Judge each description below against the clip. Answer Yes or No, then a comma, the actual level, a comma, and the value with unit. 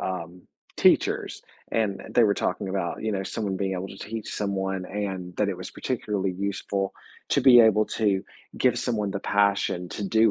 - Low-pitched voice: Yes, low, 100 Hz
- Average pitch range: No, narrow, 1.8 semitones